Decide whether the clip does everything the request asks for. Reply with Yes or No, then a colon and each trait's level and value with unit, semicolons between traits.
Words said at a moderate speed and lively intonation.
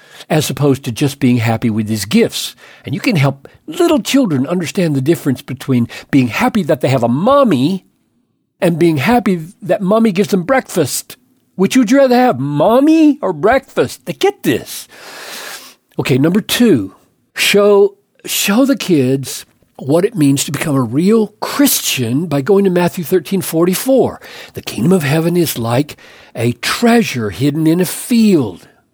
Yes: average, 165 wpm; wide, 8.1 semitones